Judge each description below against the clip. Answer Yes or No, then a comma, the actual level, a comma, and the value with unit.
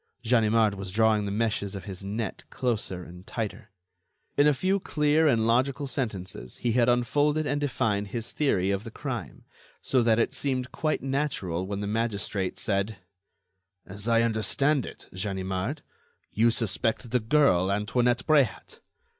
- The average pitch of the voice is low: Yes, low, 115 Hz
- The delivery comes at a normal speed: Yes, average, 155 wpm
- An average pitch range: Yes, average, 4.5 semitones